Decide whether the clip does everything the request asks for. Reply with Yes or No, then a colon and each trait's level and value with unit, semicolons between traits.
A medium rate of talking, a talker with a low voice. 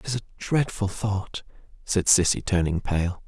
Yes: average, 165 wpm; low, 100 Hz